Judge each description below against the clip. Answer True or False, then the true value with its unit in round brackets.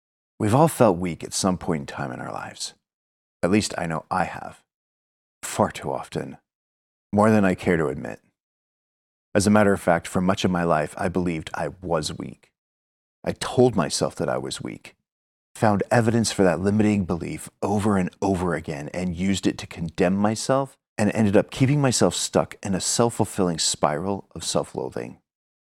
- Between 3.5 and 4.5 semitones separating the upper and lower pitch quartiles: False (4.9 semitones)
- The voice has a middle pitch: False (95 Hz)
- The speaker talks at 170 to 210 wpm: True (185 wpm)